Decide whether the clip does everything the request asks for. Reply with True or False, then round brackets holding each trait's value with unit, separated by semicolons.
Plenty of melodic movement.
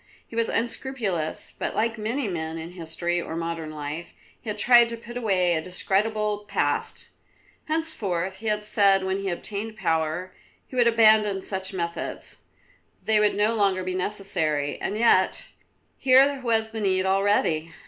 False (4.3 semitones)